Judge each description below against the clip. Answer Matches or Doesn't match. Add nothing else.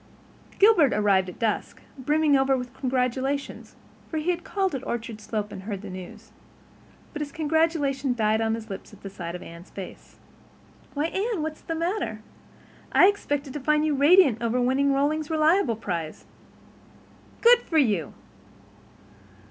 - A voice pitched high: Matches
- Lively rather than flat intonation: Matches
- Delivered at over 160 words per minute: Doesn't match